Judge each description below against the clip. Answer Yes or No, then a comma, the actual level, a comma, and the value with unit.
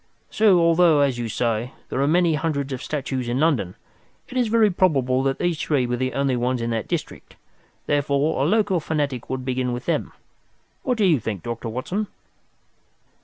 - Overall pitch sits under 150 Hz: Yes, medium, 140 Hz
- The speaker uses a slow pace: No, average, 185 wpm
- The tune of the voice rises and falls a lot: No, average, 5.0 semitones